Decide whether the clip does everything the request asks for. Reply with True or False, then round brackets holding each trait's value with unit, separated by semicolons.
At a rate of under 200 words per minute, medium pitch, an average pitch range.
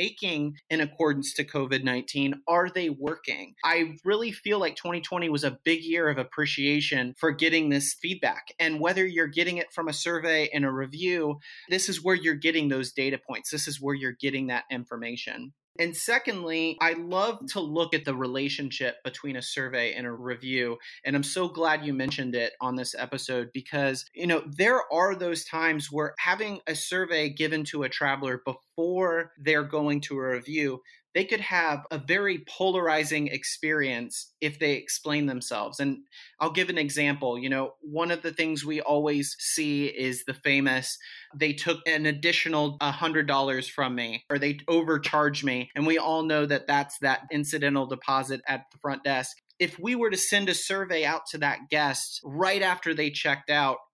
True (180 wpm; 150 Hz; 3.3 semitones)